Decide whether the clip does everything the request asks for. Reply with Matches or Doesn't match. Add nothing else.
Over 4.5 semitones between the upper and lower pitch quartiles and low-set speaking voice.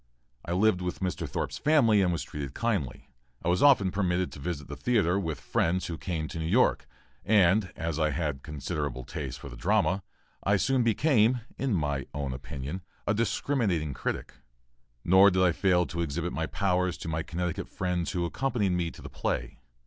Doesn't match